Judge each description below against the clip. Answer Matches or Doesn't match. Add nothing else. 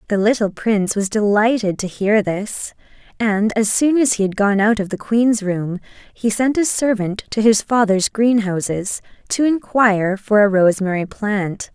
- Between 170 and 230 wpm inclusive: Matches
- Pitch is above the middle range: Matches